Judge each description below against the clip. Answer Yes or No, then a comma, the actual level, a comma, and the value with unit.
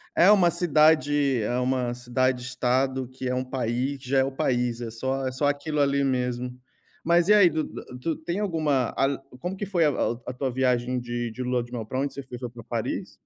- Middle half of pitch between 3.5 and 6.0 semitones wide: No, average, 2.8 semitones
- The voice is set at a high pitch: No, low, 130 Hz